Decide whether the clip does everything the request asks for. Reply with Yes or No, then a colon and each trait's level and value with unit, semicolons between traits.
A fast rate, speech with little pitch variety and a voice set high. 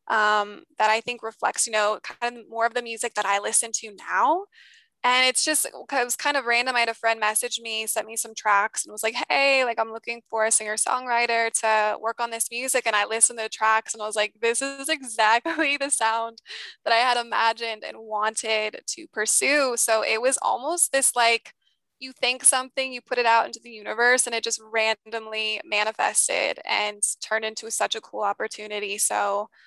Yes: fast, 210 wpm; narrow, 2.2 semitones; high, 230 Hz